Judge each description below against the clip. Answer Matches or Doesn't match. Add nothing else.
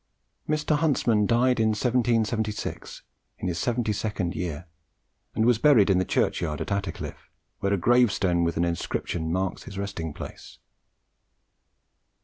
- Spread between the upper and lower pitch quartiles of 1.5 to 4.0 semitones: Doesn't match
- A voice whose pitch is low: Matches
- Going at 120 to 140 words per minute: Matches